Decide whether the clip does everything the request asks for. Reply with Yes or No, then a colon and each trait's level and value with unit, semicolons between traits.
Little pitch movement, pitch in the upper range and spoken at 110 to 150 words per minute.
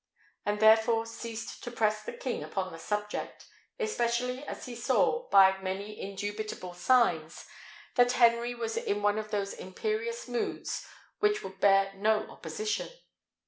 No: average, 3.6 semitones; high, 220 Hz; average, 140 wpm